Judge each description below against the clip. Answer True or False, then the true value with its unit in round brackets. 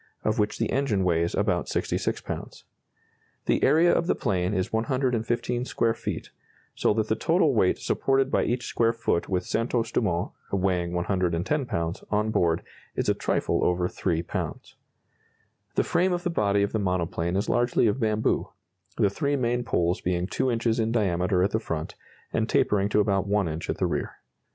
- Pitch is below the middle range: True (105 Hz)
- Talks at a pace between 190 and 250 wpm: False (180 wpm)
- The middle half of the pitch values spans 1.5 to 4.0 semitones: False (4.9 semitones)